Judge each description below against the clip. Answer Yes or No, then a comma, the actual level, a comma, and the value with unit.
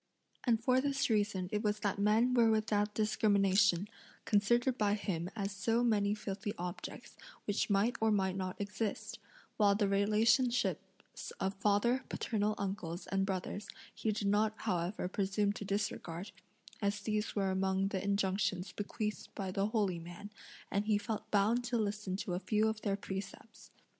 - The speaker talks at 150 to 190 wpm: Yes, average, 160 wpm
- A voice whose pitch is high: Yes, high, 205 Hz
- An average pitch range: No, narrow, 1.8 semitones